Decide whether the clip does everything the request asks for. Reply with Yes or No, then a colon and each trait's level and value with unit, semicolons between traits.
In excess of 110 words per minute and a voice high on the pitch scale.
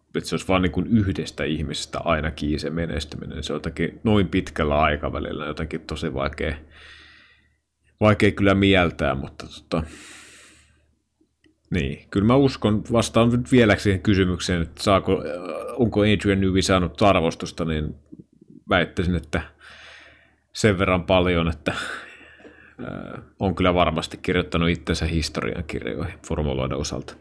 No: average, 120 wpm; very low, 90 Hz